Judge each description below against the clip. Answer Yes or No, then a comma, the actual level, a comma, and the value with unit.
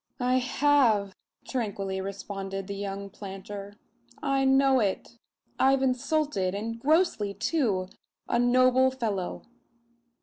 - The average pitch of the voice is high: Yes, high, 230 Hz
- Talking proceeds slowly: Yes, slow, 105 wpm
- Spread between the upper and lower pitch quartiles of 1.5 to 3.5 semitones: No, average, 4.9 semitones